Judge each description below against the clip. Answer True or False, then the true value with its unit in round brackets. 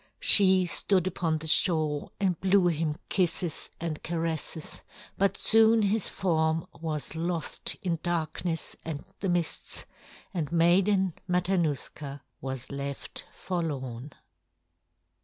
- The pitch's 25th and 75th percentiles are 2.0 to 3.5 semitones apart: True (3.1 semitones)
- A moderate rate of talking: False (110 wpm)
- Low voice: False (165 Hz)